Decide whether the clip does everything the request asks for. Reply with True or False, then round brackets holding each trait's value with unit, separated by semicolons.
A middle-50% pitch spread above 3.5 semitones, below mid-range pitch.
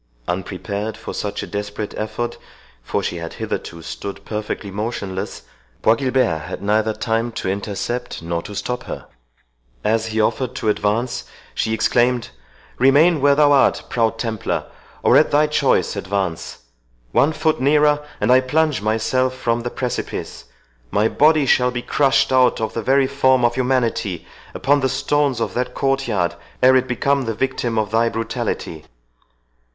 True (4.1 semitones; 120 Hz)